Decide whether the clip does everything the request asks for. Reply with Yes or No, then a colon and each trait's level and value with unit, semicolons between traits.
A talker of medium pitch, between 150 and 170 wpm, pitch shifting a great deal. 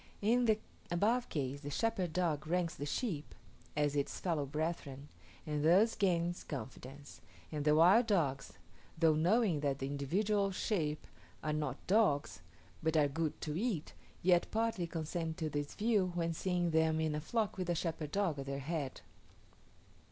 No: medium, 160 Hz; average, 165 wpm; average, 4.2 semitones